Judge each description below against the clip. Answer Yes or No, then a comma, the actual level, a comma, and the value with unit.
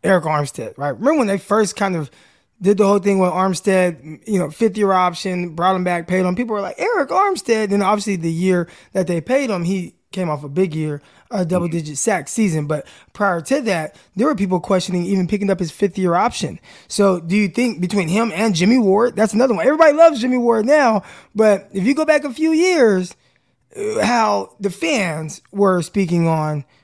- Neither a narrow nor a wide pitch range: Yes, average, 3.8 semitones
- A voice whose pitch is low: No, high, 195 Hz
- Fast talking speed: Yes, fast, 210 wpm